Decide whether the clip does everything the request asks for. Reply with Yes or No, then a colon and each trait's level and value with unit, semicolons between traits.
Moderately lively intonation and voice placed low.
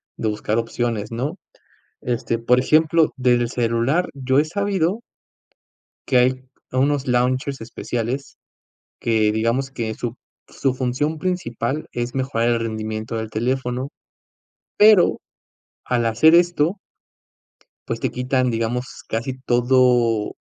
Yes: average, 3.0 semitones; low, 125 Hz